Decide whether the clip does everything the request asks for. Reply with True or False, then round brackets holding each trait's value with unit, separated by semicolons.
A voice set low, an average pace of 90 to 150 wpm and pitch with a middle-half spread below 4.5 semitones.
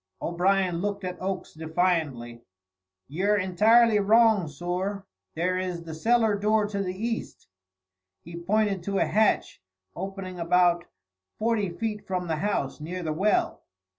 False (185 Hz; 135 wpm; 3.4 semitones)